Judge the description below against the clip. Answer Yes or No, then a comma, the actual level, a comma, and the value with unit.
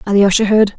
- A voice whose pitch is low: No, high, 205 Hz